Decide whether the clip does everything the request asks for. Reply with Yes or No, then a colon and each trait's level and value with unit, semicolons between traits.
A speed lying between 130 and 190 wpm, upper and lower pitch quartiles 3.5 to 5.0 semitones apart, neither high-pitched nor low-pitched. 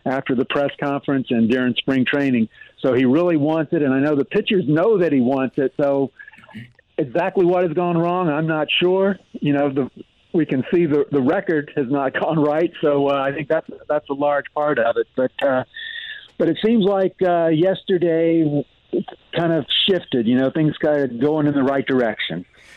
No: fast, 205 wpm; average, 4.1 semitones; medium, 150 Hz